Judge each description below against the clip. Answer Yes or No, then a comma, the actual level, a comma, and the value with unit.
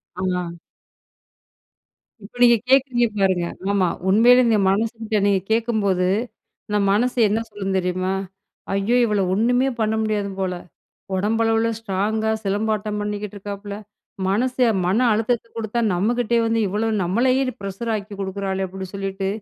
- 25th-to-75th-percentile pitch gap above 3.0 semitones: No, average, 2.7 semitones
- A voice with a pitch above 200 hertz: Yes, high, 210 Hz